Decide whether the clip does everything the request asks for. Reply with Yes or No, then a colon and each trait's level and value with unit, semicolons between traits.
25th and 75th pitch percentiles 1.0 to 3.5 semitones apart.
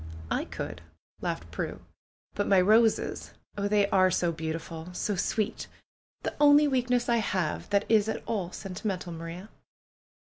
No: average, 4.1 semitones